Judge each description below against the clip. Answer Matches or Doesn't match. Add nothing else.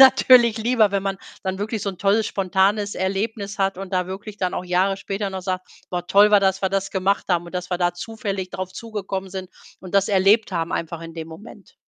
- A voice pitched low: Doesn't match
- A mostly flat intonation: Matches